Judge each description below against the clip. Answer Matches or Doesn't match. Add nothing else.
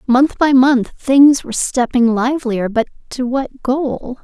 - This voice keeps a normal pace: Matches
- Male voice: Doesn't match